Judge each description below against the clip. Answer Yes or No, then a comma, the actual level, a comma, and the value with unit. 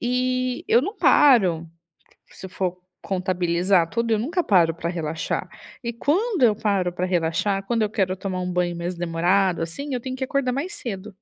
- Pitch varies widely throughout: Yes, wide, 5.9 semitones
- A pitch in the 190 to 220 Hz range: Yes, high, 195 Hz